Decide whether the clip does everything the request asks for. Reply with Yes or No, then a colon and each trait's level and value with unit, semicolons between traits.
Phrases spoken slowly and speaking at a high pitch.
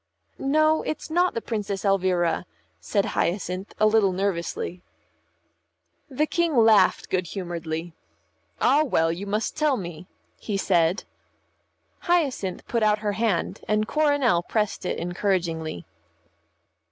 Yes: slow, 120 wpm; high, 200 Hz